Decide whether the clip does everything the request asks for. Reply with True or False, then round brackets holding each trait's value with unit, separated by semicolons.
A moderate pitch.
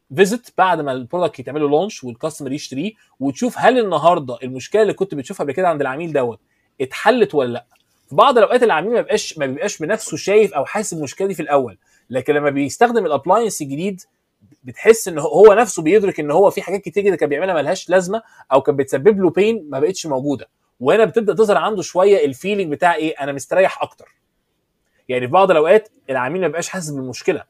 True (175 Hz)